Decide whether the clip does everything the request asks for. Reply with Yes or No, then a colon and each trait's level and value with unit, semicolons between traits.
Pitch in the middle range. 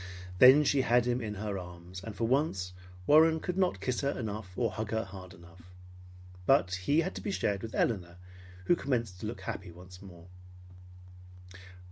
No: low, 105 Hz